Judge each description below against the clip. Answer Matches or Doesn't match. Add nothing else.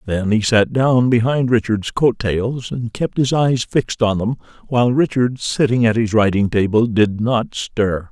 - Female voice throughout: Doesn't match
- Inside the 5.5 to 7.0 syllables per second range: Doesn't match